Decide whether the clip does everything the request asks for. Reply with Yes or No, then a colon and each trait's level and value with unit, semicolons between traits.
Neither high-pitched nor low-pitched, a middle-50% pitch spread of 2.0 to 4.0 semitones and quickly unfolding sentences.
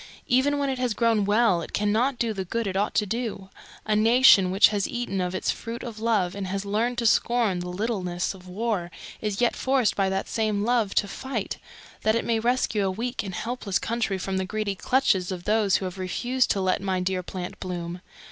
No: high, 210 Hz; average, 3.6 semitones; fast, 220 wpm